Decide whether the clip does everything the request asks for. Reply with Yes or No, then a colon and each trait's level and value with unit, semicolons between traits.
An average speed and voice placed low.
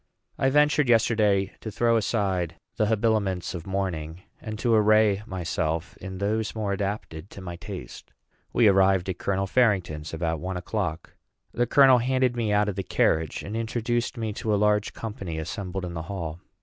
Yes: average, 175 wpm; low, 100 Hz